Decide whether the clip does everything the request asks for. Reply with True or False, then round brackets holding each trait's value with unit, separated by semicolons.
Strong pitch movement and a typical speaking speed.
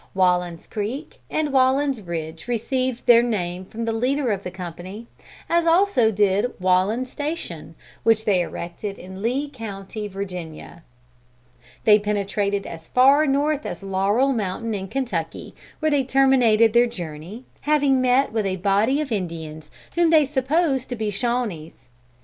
True (5.9 semitones; 150 wpm)